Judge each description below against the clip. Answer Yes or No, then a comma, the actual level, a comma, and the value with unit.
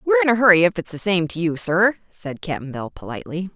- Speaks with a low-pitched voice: No, medium, 185 Hz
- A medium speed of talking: No, fast, 255 wpm